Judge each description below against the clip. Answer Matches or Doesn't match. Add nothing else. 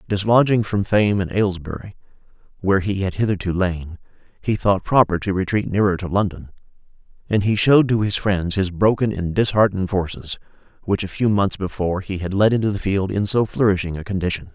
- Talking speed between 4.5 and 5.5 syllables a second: Doesn't match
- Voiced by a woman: Doesn't match